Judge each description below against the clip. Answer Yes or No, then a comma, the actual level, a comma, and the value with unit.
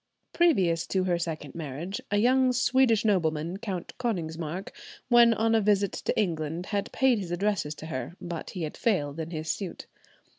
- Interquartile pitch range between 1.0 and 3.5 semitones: No, average, 5.2 semitones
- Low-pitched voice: No, medium, 185 Hz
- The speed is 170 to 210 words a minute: Yes, average, 175 wpm